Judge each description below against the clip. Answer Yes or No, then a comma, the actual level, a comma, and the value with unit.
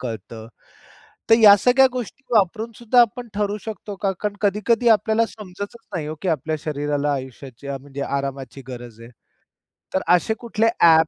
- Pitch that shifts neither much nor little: No, wide, 7.9 semitones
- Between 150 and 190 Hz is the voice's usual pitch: Yes, medium, 185 Hz